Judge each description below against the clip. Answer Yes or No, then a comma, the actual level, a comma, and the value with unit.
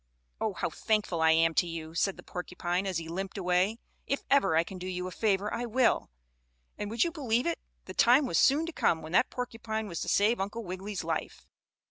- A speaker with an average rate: No, fast, 220 wpm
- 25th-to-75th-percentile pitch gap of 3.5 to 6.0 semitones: Yes, average, 4.7 semitones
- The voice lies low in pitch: No, high, 195 Hz